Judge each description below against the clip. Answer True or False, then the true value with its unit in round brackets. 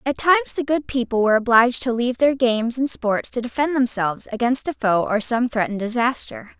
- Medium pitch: False (240 Hz)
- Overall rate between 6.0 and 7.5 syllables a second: True (6.1 syllables/s)